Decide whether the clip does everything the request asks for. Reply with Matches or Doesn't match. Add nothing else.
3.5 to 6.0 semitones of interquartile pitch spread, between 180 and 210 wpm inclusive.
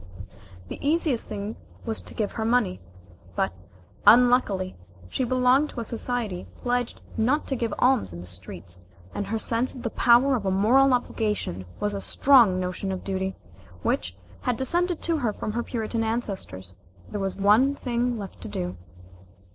Doesn't match